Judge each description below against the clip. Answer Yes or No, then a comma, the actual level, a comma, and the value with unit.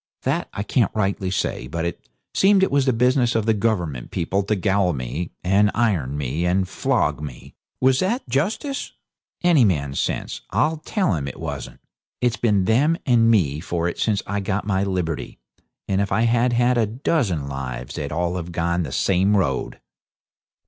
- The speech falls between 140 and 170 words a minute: No, average, 185 wpm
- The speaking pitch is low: Yes, low, 100 Hz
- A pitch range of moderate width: No, wide, 6.0 semitones